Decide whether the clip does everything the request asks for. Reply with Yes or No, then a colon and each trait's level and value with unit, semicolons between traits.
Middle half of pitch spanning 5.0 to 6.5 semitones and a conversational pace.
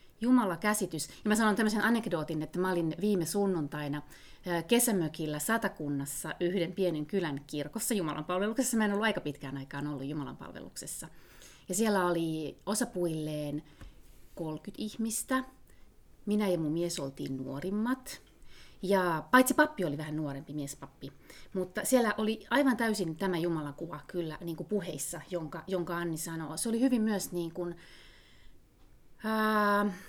Yes: wide, 5.5 semitones; average, 140 wpm